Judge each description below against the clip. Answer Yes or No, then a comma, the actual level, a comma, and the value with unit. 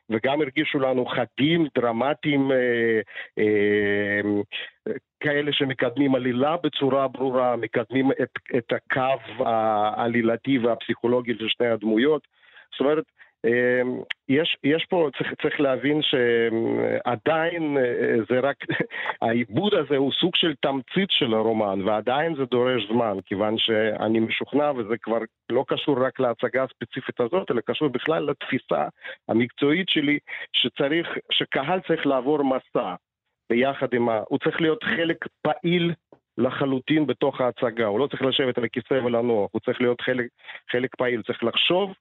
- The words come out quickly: No, average, 135 wpm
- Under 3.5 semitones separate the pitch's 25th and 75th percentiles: No, average, 4.0 semitones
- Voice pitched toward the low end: Yes, low, 130 Hz